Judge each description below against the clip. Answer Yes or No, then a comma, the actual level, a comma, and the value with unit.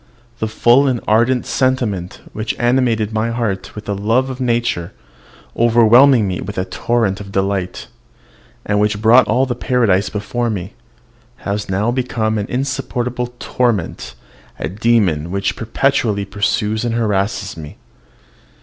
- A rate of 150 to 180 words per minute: No, slow, 135 wpm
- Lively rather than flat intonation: No, average, 3.2 semitones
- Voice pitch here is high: No, low, 110 Hz